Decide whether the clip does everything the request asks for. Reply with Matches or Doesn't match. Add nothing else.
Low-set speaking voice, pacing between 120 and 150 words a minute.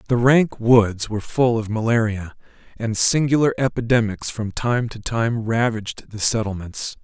Matches